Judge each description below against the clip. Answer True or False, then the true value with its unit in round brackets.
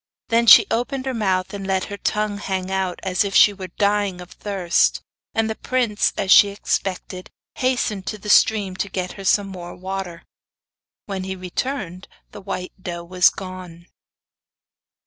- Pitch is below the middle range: False (195 Hz)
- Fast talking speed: False (165 wpm)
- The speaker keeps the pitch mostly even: True (2.1 semitones)